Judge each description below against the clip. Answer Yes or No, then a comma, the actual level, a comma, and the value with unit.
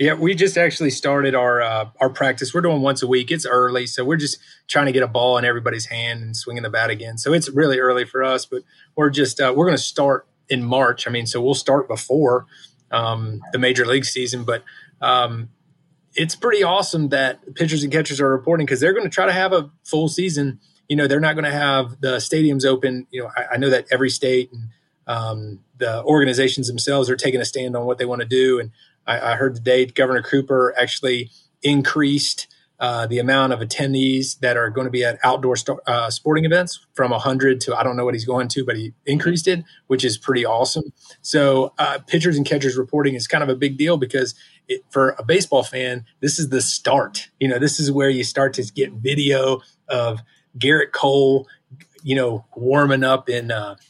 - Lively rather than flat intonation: No, average, 2.7 semitones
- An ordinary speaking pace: No, fast, 220 wpm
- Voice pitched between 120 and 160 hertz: Yes, low, 130 Hz